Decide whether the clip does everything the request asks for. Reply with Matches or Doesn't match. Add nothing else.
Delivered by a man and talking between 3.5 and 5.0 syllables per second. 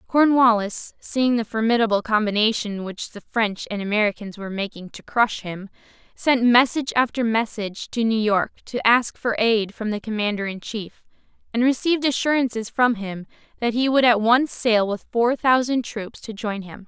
Doesn't match